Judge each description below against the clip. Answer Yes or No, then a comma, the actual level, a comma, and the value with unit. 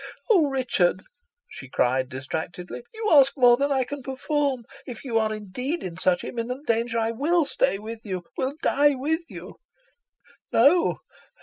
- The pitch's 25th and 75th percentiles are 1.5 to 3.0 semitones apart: No, average, 5.0 semitones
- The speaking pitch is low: No, very high, 250 Hz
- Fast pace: No, average, 160 wpm